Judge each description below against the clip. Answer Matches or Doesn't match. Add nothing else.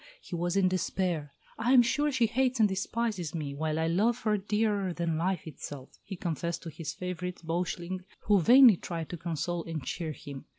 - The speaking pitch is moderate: Matches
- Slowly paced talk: Doesn't match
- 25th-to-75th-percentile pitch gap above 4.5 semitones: Doesn't match